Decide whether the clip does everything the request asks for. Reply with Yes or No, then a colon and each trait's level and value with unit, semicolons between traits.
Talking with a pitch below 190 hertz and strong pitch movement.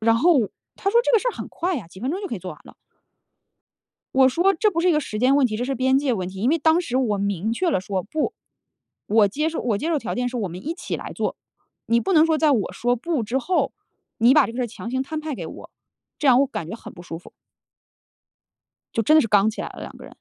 No: very high, 255 Hz; wide, 6.3 semitones